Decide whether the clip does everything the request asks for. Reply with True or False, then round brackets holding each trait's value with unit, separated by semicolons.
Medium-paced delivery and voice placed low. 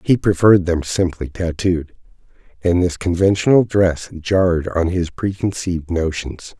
False (125 wpm; 90 Hz)